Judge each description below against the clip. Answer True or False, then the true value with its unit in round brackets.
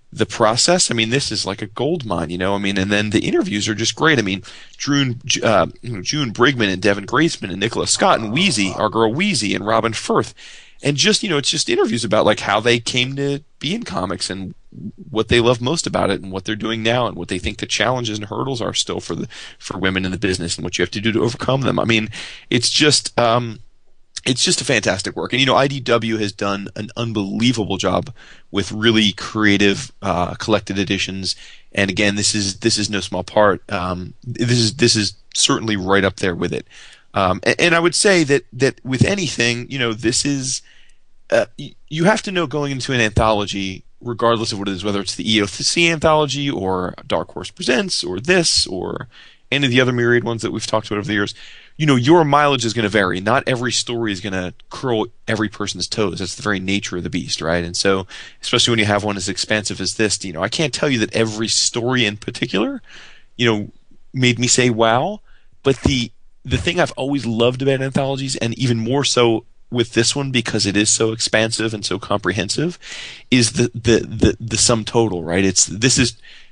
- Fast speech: True (220 wpm)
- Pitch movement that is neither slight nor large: True (4.1 semitones)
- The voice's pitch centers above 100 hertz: True (115 Hz)